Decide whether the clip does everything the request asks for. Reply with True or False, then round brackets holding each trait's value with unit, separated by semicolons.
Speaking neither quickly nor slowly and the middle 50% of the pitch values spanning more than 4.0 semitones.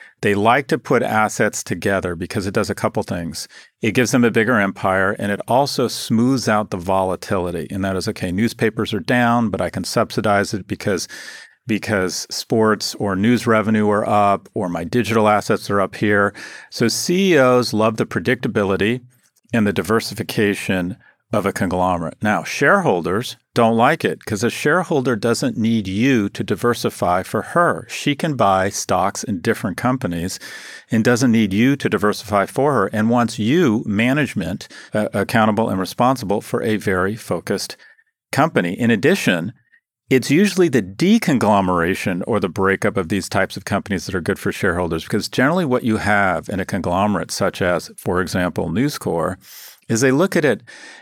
False (170 wpm; 3.3 semitones)